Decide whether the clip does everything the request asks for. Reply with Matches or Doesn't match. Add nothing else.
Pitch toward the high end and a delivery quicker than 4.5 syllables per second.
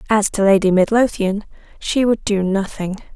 Matches